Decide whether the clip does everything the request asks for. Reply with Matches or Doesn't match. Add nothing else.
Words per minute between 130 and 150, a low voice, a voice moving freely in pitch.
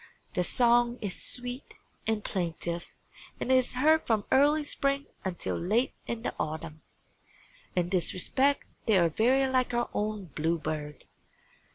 Doesn't match